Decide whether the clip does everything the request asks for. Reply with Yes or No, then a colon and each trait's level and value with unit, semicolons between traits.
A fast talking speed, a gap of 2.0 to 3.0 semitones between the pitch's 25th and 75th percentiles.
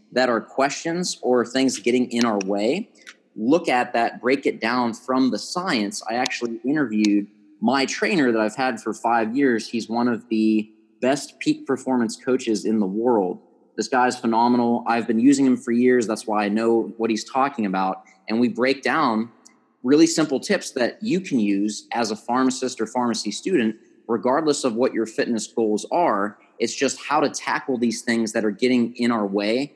No: average, 190 wpm; narrow, 2.6 semitones